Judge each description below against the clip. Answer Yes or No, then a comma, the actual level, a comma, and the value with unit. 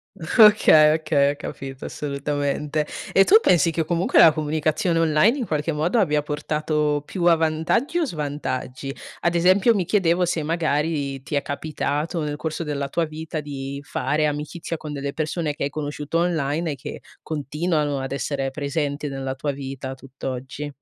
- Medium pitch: Yes, medium, 150 Hz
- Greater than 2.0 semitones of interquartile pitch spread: Yes, narrow, 2.6 semitones